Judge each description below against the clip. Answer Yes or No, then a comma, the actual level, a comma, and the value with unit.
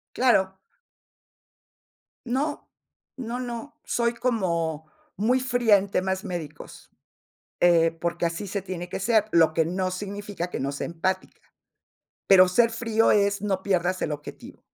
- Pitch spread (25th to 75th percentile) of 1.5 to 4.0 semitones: No, average, 4.7 semitones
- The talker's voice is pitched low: No, high, 190 Hz